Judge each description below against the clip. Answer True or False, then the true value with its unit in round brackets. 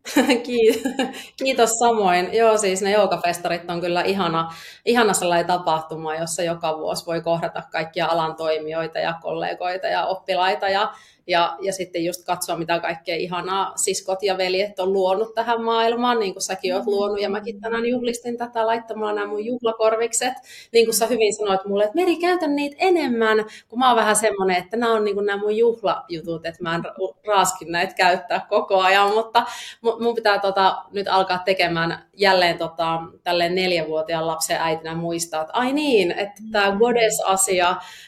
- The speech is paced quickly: True (165 wpm)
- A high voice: True (195 Hz)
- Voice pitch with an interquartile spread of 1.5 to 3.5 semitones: False (4.7 semitones)